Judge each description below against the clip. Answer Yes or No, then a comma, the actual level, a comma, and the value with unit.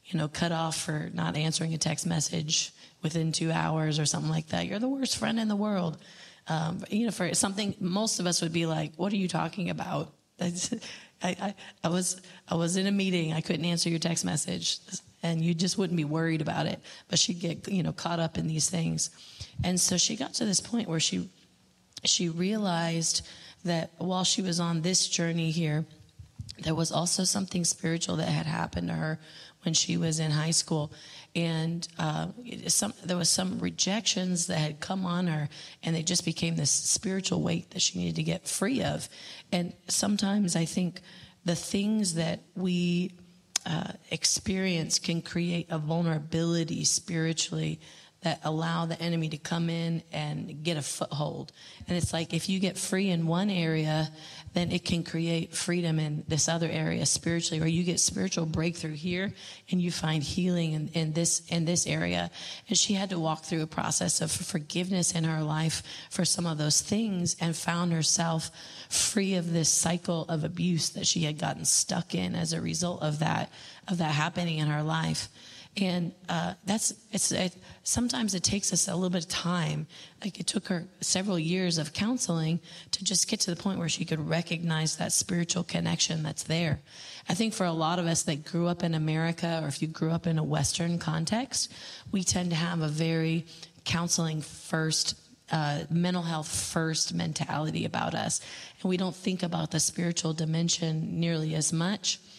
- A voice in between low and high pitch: Yes, medium, 170 Hz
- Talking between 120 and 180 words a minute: No, average, 190 wpm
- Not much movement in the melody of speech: Yes, narrow, 2.2 semitones